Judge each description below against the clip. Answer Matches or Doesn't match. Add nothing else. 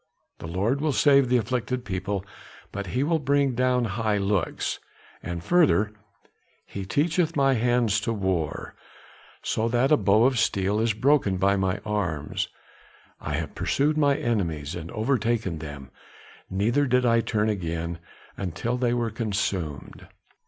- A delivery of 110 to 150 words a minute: Matches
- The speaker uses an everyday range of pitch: Matches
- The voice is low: Matches